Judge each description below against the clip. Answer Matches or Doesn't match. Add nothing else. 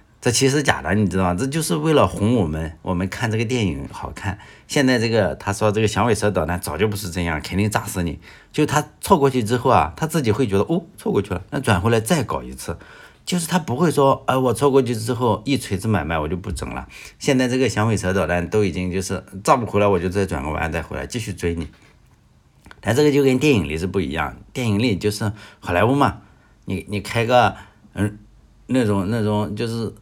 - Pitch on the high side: Doesn't match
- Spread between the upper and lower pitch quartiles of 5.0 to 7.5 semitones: Matches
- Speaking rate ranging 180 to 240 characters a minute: Doesn't match